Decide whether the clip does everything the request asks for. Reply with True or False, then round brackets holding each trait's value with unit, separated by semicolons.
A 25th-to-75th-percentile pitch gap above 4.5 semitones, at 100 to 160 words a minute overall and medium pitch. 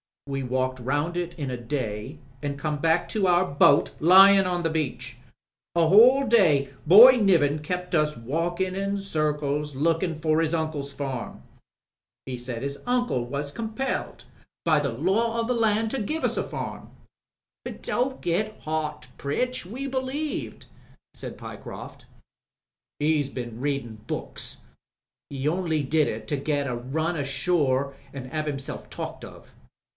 True (5.3 semitones; 155 wpm; 155 Hz)